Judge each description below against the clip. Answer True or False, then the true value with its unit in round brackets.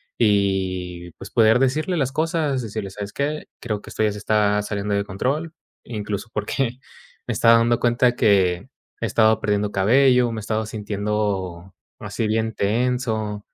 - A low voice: True (110 Hz)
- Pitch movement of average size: True (3.2 semitones)